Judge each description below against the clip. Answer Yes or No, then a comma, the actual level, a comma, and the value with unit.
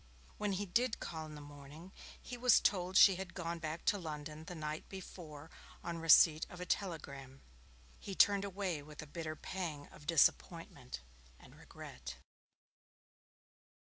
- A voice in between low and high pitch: Yes, medium, 165 Hz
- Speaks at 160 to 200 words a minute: No, average, 150 wpm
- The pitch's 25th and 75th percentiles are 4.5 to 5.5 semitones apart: No, average, 3.9 semitones